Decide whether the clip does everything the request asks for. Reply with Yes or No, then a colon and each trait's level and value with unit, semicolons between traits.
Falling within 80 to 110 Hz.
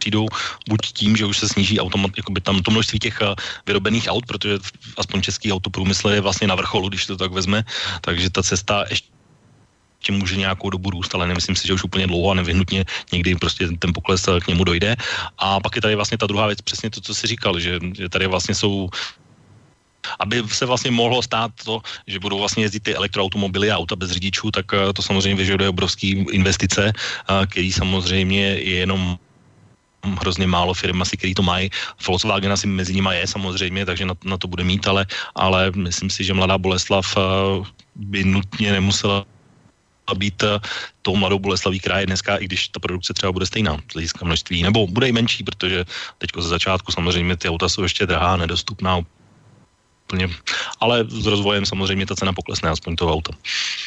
Yes: very low, 95 Hz